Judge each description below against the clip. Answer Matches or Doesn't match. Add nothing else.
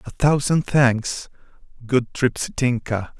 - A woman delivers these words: Doesn't match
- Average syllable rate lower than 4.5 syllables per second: Matches